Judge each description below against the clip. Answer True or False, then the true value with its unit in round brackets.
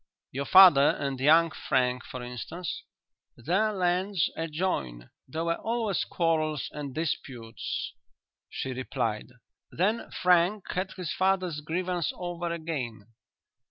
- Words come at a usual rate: False (115 wpm)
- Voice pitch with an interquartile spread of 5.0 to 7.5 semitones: True (5.4 semitones)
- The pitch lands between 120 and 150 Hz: False (165 Hz)